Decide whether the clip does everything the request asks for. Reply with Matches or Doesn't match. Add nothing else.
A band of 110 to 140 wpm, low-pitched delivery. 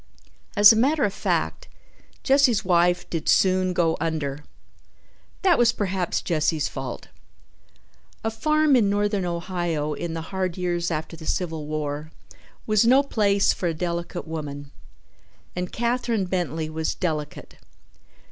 Doesn't match